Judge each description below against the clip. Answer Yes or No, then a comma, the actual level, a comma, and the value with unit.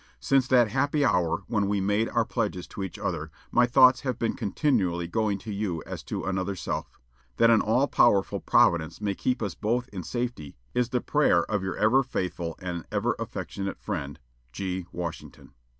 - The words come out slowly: No, average, 180 wpm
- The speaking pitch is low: Yes, low, 105 Hz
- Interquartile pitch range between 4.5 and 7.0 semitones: Yes, average, 5.0 semitones